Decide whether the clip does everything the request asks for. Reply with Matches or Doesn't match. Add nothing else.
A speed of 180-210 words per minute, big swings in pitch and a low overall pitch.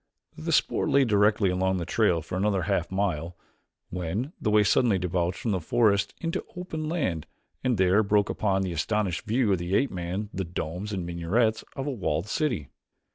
Doesn't match